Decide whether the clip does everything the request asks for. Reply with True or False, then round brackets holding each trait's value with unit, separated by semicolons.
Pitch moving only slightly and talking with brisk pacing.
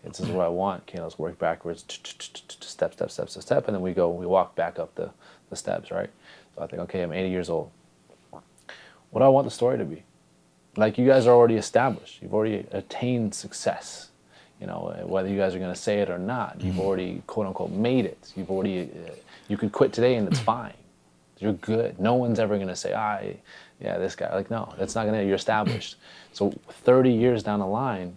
False (3.9 semitones; 225 wpm)